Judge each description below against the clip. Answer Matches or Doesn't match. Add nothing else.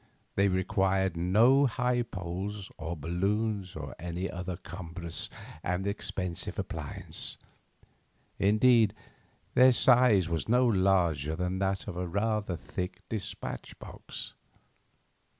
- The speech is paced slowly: Matches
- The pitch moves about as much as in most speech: Matches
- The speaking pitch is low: Matches